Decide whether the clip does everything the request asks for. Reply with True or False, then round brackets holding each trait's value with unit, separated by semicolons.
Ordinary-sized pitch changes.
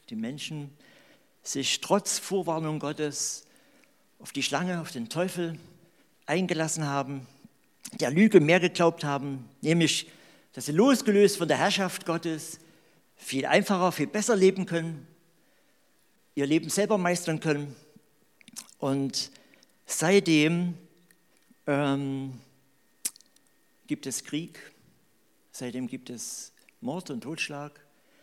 True (4.2 semitones)